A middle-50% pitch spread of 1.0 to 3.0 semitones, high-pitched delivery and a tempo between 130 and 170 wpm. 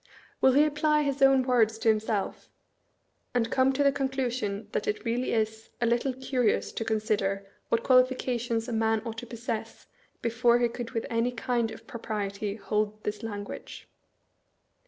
Yes: narrow, 2.5 semitones; high, 230 Hz; average, 160 wpm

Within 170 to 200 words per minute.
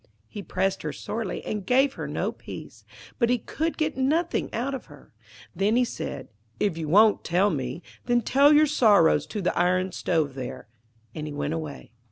Yes: average, 190 wpm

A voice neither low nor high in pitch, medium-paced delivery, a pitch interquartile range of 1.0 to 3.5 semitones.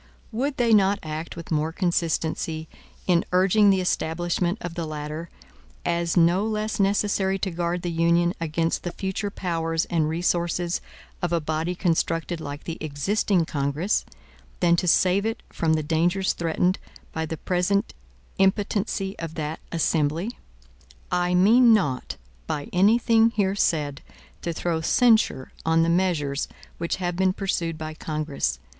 Yes: medium, 170 Hz; average, 150 wpm; average, 3.1 semitones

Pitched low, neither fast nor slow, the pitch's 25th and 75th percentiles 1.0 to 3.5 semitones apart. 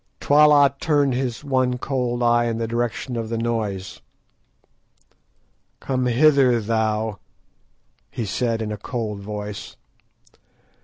No: low, 120 Hz; slow, 115 wpm; average, 2.8 semitones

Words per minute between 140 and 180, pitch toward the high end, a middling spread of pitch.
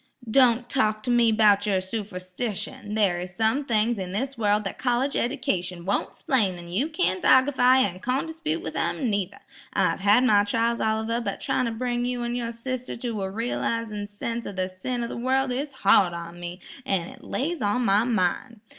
No: average, 195 wpm; high, 225 Hz; average, 4.1 semitones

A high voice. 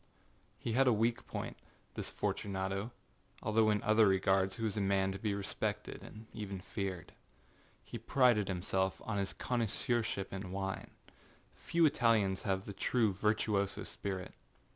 No: low, 100 Hz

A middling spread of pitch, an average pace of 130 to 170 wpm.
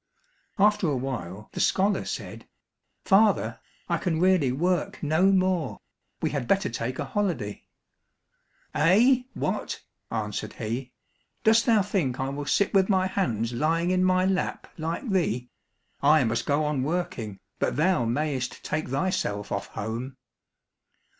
No: wide, 7.1 semitones; average, 140 wpm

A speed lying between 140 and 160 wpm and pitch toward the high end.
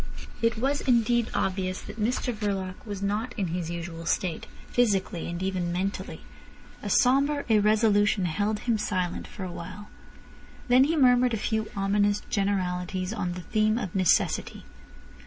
Yes: average, 150 wpm; high, 205 Hz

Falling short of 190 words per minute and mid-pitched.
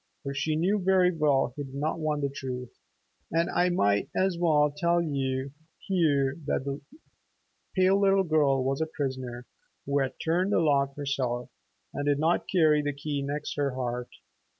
Yes: average, 175 wpm; medium, 145 Hz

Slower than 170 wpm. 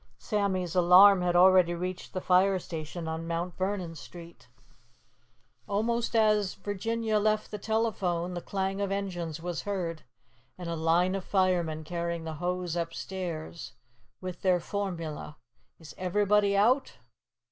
Yes: slow, 135 wpm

